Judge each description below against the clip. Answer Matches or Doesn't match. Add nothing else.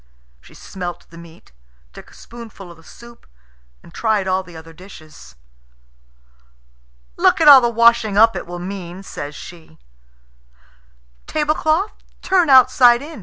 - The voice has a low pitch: Doesn't match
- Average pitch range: Doesn't match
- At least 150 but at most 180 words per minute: Doesn't match